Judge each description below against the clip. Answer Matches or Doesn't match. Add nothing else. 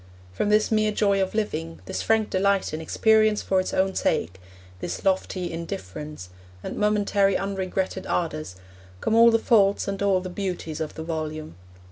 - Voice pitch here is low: Doesn't match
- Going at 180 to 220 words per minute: Doesn't match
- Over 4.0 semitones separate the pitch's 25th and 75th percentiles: Matches